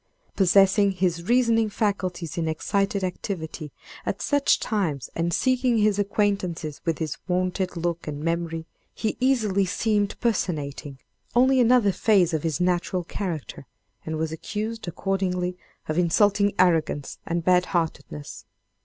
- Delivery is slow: Yes, slow, 130 wpm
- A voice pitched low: No, medium, 185 Hz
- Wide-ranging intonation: No, average, 3.8 semitones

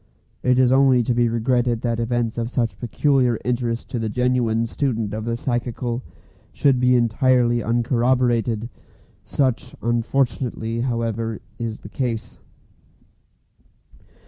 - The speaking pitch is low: Yes, low, 120 Hz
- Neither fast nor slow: No, slow, 120 wpm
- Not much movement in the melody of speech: Yes, narrow, 1.5 semitones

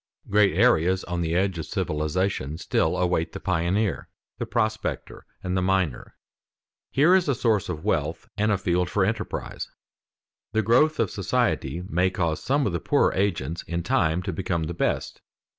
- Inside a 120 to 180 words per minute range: Yes, average, 170 wpm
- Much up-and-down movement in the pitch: No, average, 3.8 semitones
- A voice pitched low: Yes, very low, 95 Hz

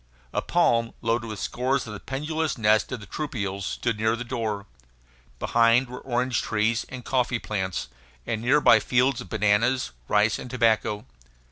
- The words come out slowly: No, average, 165 wpm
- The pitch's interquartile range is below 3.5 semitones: Yes, average, 2.9 semitones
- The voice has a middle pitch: No, low, 115 Hz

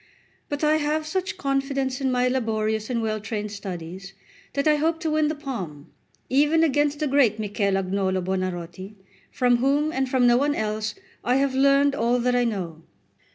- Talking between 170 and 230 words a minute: Yes, average, 180 wpm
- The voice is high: Yes, very high, 250 Hz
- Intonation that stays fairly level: No, wide, 5.5 semitones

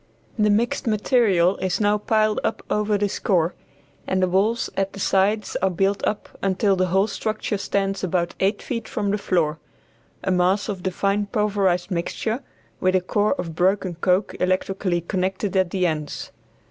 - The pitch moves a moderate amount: No, narrow, 2.2 semitones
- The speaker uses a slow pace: No, average, 170 wpm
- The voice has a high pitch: Yes, high, 195 Hz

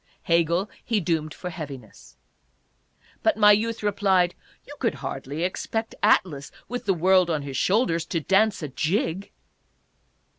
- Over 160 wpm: No, average, 145 wpm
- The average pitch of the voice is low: No, medium, 180 Hz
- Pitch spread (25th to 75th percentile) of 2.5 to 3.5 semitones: No, average, 4.4 semitones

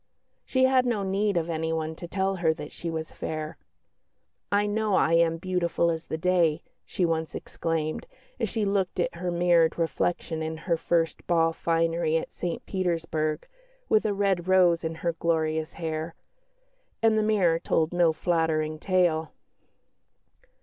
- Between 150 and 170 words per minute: Yes, average, 155 wpm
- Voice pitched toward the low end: No, medium, 170 Hz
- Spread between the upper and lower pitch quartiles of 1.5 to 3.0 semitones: Yes, narrow, 2.4 semitones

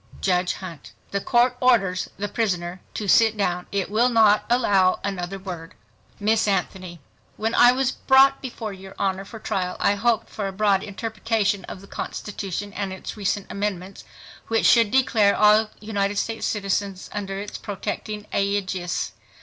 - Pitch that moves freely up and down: No, narrow, 2.6 semitones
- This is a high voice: Yes, high, 200 Hz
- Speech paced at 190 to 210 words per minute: No, average, 150 wpm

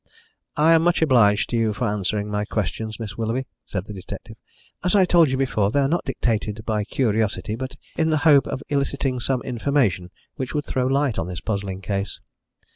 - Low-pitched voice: Yes, low, 115 Hz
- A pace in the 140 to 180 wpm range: No, average, 200 wpm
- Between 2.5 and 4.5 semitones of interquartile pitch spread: No, average, 5.1 semitones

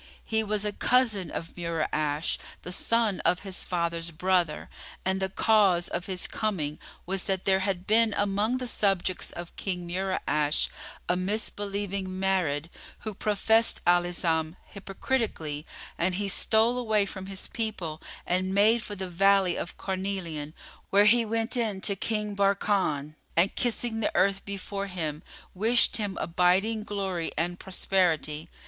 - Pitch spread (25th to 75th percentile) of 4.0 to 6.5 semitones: No, average, 3.0 semitones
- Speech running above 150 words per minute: No, average, 145 wpm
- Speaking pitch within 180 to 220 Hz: Yes, high, 190 Hz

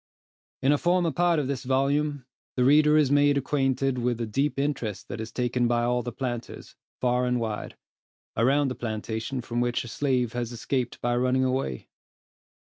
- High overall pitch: No, low, 125 Hz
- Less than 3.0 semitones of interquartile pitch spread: Yes, narrow, 2.6 semitones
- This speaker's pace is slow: No, average, 180 wpm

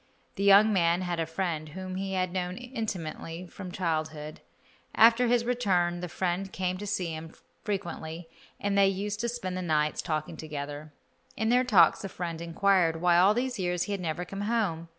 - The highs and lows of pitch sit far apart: No, average, 3.3 semitones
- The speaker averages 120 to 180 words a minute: No, average, 190 wpm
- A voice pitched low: No, medium, 180 Hz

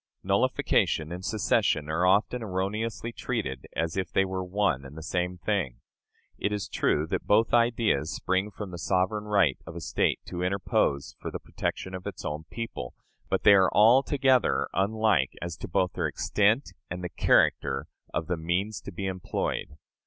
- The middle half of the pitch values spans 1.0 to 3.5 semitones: No, average, 4.2 semitones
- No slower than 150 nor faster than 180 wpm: Yes, average, 175 wpm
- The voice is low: Yes, very low, 95 Hz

